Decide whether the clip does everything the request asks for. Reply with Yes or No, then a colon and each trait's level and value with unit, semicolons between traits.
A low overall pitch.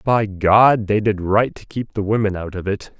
Yes: low, 105 Hz